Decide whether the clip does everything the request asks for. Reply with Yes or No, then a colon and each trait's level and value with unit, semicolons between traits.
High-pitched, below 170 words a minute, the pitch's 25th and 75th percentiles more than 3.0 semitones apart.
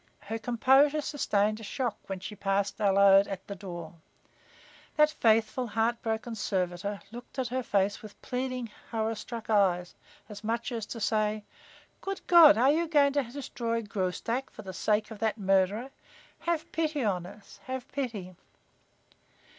Yes: high, 220 Hz; average, 155 wpm; average, 4.1 semitones